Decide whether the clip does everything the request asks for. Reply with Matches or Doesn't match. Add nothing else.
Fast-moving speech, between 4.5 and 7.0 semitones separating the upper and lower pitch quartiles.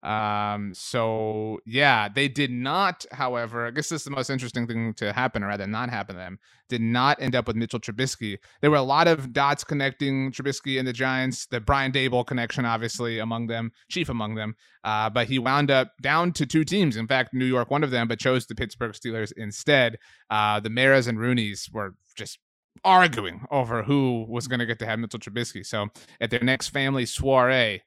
Doesn't match